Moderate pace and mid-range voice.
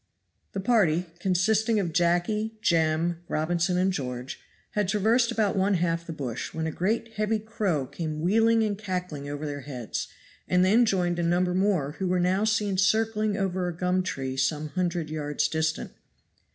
Yes: average, 170 wpm; medium, 180 Hz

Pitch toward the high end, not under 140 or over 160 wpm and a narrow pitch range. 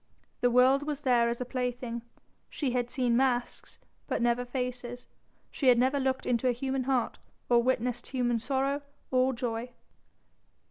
Yes: very high, 250 Hz; average, 155 wpm; narrow, 1.5 semitones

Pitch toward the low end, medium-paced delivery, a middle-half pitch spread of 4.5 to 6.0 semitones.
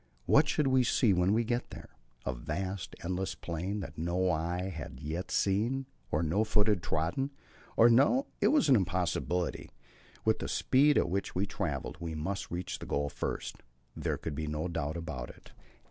Yes: very low, 90 Hz; average, 190 wpm; average, 5.2 semitones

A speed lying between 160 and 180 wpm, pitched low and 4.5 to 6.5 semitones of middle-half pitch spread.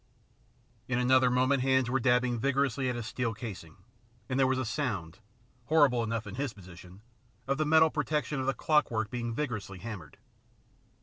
No: average, 170 wpm; low, 125 Hz; average, 3.4 semitones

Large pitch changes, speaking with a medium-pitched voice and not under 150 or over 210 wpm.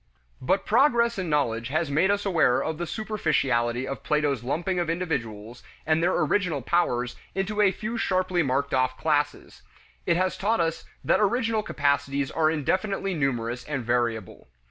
Yes: wide, 6.3 semitones; medium, 155 Hz; average, 160 wpm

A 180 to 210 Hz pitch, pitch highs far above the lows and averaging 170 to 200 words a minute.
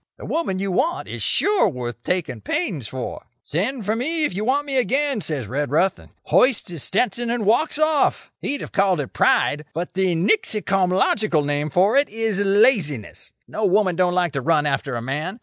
Yes: high, 190 Hz; wide, 7.7 semitones; average, 190 wpm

